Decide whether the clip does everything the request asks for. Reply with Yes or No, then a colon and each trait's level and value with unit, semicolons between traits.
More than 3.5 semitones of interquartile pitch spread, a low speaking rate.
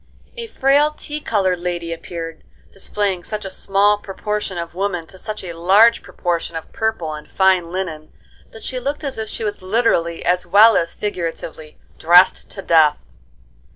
No: average, 4.0 semitones; average, 165 wpm